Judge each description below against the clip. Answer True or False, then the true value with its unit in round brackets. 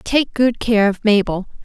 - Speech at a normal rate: True (185 wpm)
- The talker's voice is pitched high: True (220 Hz)